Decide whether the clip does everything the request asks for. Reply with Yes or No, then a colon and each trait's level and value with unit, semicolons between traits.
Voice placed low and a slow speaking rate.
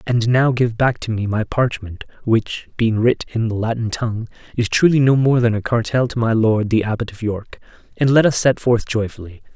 No: low, 115 Hz; fast, 205 wpm